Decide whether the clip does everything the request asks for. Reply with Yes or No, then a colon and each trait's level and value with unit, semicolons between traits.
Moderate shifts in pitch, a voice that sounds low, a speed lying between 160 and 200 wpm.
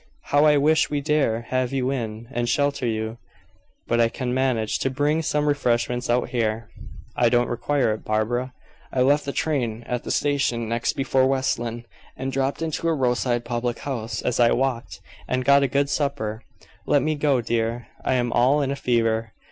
Yes: average, 3.1 semitones; low, 125 Hz; average, 190 wpm